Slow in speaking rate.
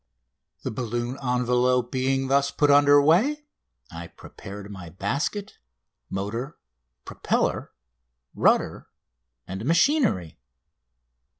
Yes: slow, 90 wpm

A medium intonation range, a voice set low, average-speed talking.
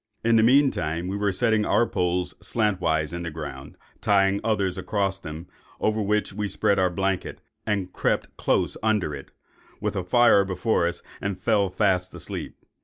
Yes: average, 3.0 semitones; very low, 95 Hz; average, 170 wpm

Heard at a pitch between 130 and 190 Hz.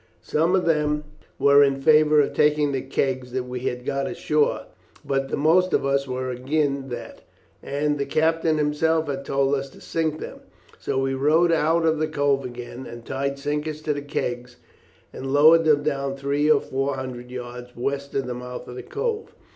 Yes: medium, 140 Hz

